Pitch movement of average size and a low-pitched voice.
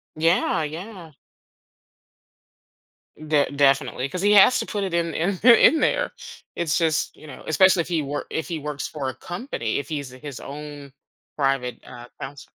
No: average, 3.9 semitones; medium, 155 Hz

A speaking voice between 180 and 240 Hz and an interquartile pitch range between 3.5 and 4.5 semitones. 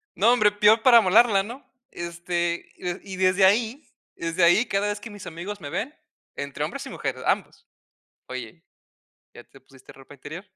Yes: high, 190 Hz; average, 3.9 semitones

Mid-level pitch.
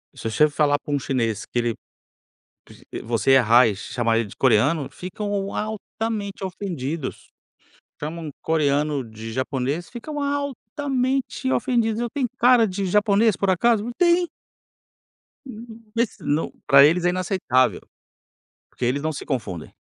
Yes: medium, 170 Hz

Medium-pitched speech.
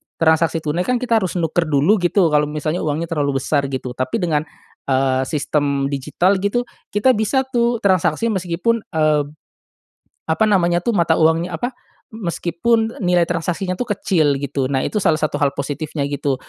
Yes: medium, 165 Hz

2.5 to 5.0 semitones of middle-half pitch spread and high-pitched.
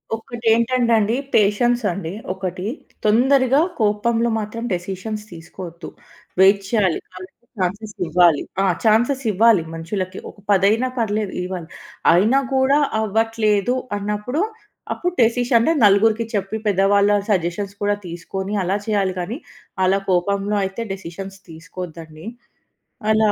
Yes: average, 3.4 semitones; high, 205 Hz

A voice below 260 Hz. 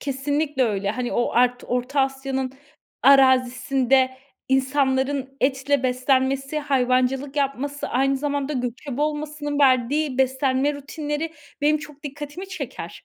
No: very high, 270 Hz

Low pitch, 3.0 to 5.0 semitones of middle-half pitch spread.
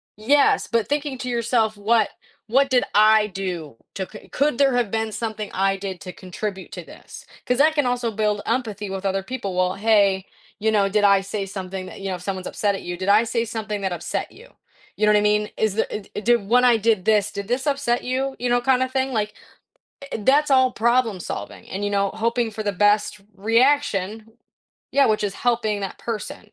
No: high, 215 Hz; average, 3.6 semitones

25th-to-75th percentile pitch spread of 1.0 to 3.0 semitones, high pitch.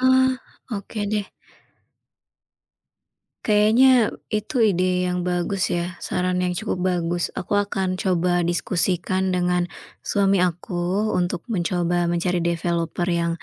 No: narrow, 2.4 semitones; medium, 180 Hz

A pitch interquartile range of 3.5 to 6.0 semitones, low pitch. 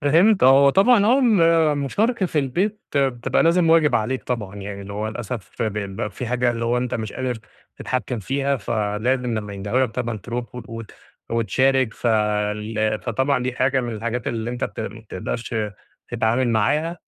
Yes: average, 3.8 semitones; low, 120 Hz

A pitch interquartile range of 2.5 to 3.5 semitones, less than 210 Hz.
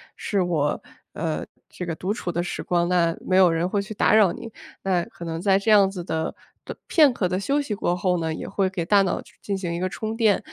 Yes: average, 2.9 semitones; medium, 185 Hz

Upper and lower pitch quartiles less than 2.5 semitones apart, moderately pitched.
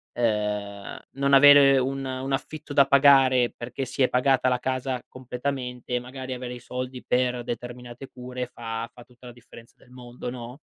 No: narrow, 1.5 semitones; low, 125 Hz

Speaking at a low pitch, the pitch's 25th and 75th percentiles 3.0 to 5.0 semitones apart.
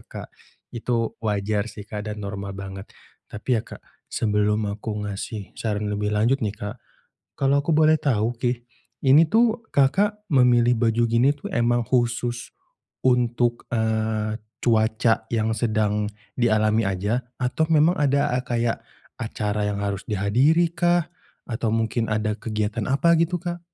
Yes: low, 115 Hz; average, 3.3 semitones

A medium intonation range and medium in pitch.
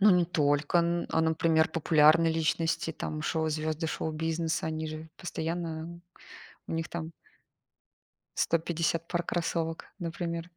No: narrow, 1.1 semitones; medium, 165 Hz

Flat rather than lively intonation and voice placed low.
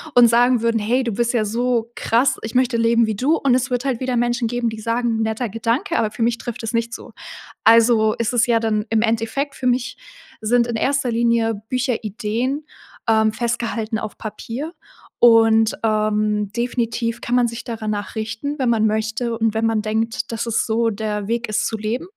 No: narrow, 1.7 semitones; high, 230 Hz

